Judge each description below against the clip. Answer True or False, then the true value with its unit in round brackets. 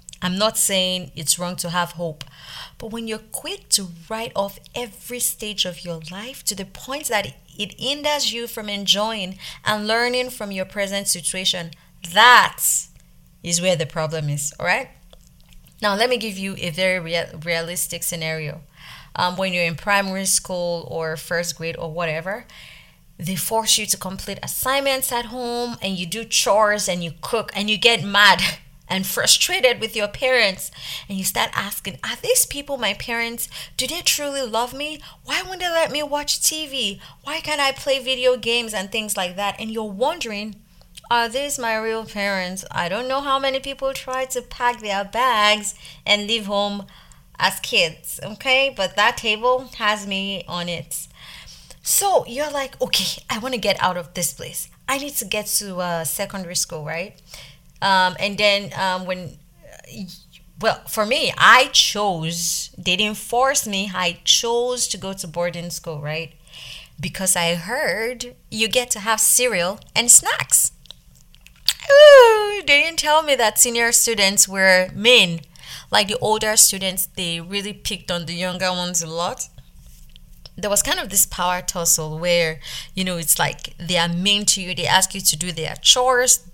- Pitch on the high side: True (200 Hz)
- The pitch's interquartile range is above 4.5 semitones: True (5.2 semitones)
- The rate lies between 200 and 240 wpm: False (175 wpm)